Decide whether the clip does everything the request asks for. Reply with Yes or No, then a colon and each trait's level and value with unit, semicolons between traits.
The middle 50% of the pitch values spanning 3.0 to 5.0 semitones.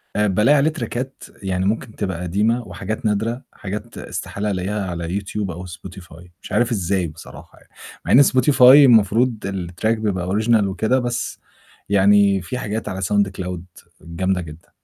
Yes: average, 3.9 semitones